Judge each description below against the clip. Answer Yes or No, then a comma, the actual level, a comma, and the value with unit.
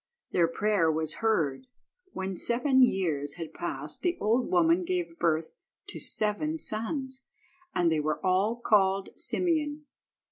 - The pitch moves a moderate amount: No, wide, 6.3 semitones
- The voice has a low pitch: No, high, 190 Hz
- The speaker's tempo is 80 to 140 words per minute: Yes, slow, 135 wpm